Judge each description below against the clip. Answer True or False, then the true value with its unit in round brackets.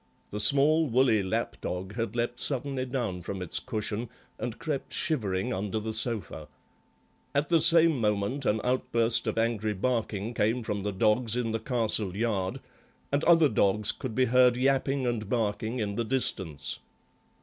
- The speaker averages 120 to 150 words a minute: False (160 wpm)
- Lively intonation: False (3.6 semitones)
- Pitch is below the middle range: True (115 Hz)